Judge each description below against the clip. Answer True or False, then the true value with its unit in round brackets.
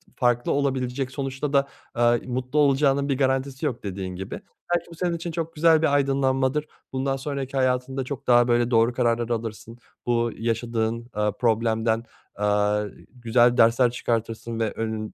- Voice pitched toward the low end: True (125 Hz)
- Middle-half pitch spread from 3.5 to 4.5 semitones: False (3.0 semitones)